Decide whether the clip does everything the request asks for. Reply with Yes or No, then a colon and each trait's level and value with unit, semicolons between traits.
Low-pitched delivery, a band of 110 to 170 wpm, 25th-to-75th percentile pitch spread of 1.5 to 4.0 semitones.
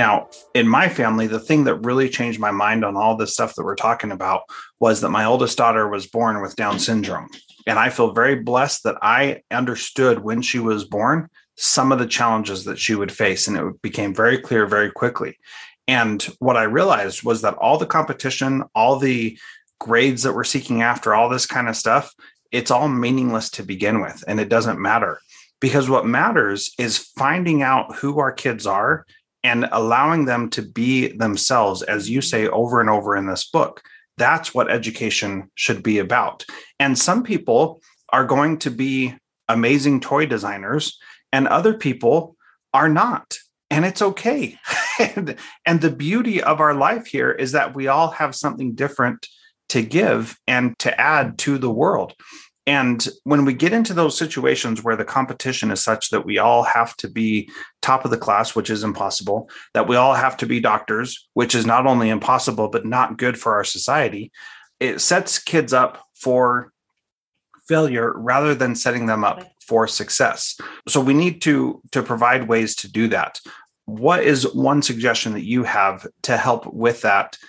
No: low, 125 Hz; average, 180 wpm; average, 3.7 semitones